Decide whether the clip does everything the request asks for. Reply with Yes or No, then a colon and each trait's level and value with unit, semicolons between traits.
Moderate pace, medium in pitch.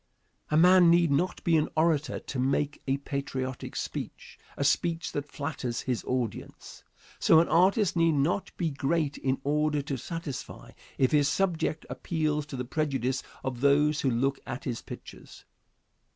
Yes: average, 160 wpm; medium, 145 Hz